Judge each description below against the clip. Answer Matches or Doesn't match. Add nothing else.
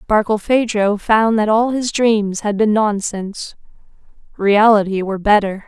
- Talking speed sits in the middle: Doesn't match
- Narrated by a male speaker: Doesn't match